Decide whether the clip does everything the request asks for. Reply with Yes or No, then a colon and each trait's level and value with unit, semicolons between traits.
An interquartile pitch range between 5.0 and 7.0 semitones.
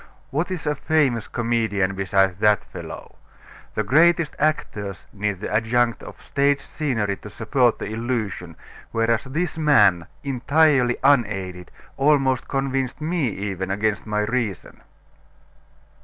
Yes: wide, 5.4 semitones